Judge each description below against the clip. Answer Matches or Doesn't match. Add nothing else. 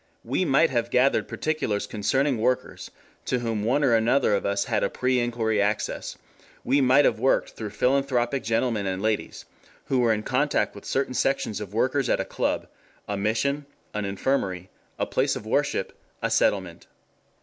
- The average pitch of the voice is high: Doesn't match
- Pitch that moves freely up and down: Doesn't match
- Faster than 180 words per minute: Doesn't match